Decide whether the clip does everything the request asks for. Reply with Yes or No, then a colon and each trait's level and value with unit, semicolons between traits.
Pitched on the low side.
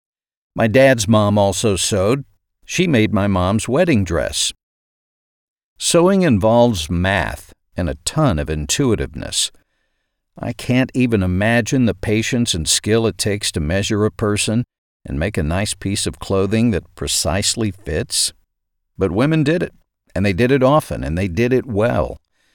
Yes: low, 105 Hz